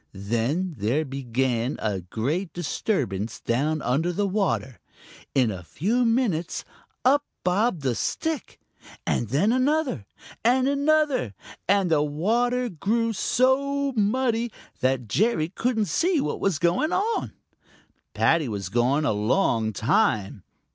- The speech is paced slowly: Yes, slow, 120 wpm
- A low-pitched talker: No, medium, 175 Hz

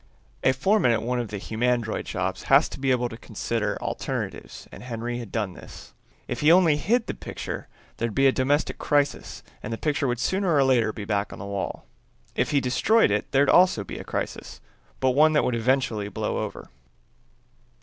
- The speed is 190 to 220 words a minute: Yes, average, 200 wpm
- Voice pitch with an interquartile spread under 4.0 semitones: No, average, 4.4 semitones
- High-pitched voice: No, low, 125 Hz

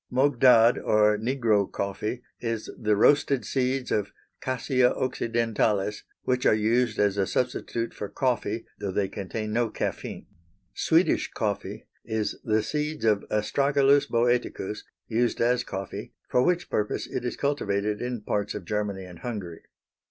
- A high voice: No, low, 115 Hz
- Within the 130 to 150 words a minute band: Yes, average, 140 wpm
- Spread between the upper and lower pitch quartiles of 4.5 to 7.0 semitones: No, average, 3.2 semitones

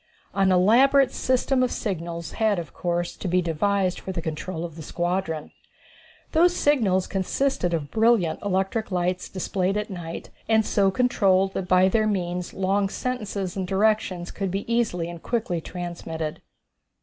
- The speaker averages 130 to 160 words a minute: Yes, average, 155 wpm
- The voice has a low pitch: No, high, 190 Hz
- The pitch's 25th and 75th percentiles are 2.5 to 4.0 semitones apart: Yes, average, 3.6 semitones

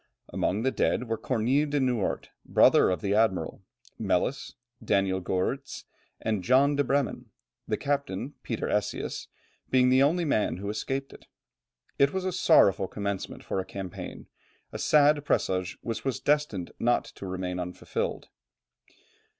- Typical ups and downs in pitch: No, wide, 6.5 semitones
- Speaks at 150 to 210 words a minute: No, average, 140 wpm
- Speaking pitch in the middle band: No, low, 115 Hz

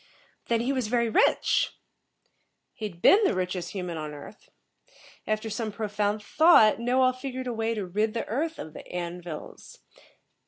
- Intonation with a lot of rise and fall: No, average, 5.0 semitones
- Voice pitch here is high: Yes, high, 215 Hz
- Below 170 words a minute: Yes, average, 160 wpm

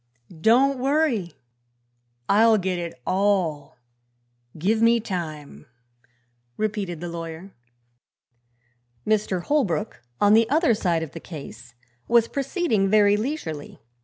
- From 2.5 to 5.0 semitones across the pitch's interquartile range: No, wide, 5.5 semitones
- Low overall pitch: No, high, 200 Hz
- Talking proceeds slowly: Yes, slow, 105 wpm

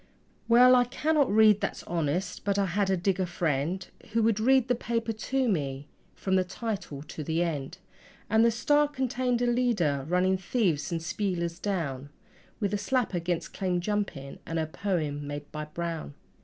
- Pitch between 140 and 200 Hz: Yes, high, 190 Hz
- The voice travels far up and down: Yes, wide, 5.8 semitones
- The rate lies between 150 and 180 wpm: Yes, average, 175 wpm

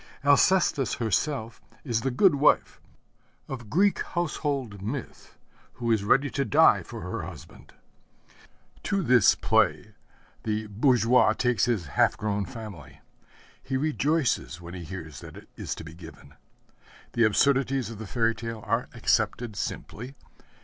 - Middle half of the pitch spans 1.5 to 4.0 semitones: No, average, 4.7 semitones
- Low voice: Yes, low, 115 Hz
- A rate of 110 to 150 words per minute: Yes, average, 140 wpm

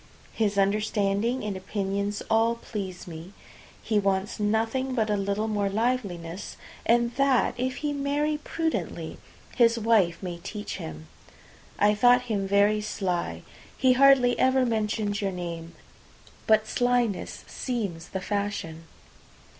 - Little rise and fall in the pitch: No, average, 3.7 semitones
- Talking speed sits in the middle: No, slow, 130 wpm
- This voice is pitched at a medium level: No, high, 210 Hz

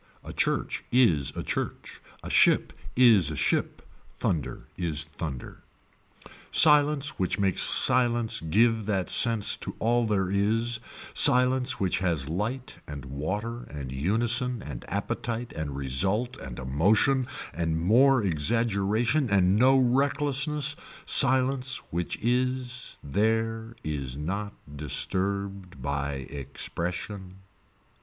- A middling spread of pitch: No, wide, 7.2 semitones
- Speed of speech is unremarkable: No, slow, 115 wpm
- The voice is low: Yes, low, 105 Hz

